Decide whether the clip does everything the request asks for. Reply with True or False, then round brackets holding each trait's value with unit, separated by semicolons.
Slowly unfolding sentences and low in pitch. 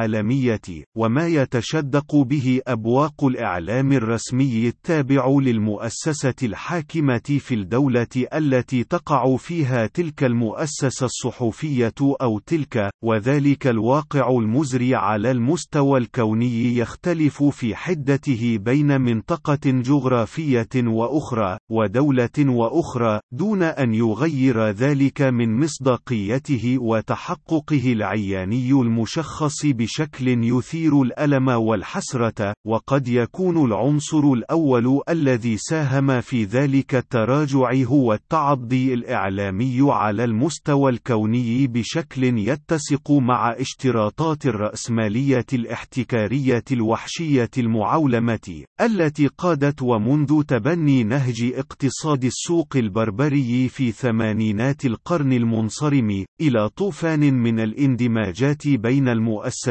False (90 wpm; 130 Hz)